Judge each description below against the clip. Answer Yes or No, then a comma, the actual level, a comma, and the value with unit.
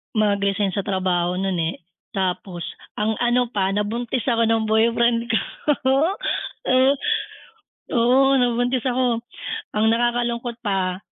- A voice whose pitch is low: No, high, 225 Hz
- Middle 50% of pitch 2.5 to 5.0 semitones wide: Yes, average, 3.7 semitones